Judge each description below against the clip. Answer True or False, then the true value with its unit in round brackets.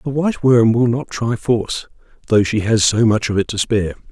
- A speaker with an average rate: False (235 wpm)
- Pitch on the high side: False (115 Hz)